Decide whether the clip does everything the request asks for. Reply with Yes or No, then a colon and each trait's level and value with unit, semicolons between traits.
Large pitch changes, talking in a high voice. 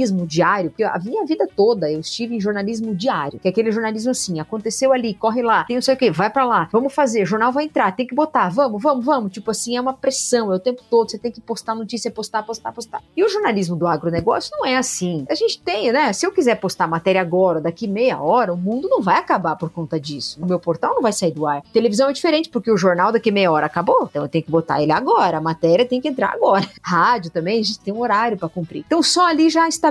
Yes: wide, 6.2 semitones; high, 225 Hz